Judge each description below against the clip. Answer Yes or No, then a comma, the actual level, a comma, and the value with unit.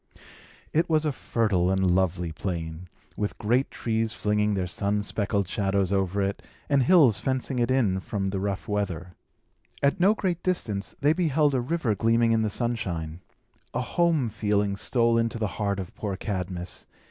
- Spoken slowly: No, average, 170 wpm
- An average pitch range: Yes, average, 4.6 semitones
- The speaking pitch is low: Yes, low, 105 Hz